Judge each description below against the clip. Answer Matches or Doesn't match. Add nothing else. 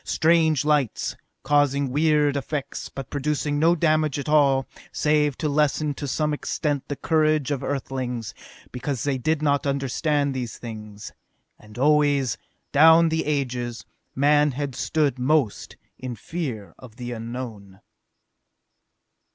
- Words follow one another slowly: Matches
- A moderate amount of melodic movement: Matches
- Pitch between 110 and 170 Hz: Matches